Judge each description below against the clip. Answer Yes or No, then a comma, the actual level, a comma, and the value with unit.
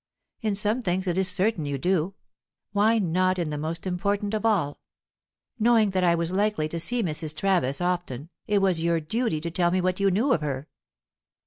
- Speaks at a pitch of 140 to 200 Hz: Yes, medium, 185 Hz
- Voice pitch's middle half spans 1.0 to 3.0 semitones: No, average, 3.7 semitones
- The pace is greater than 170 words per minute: Yes, average, 200 wpm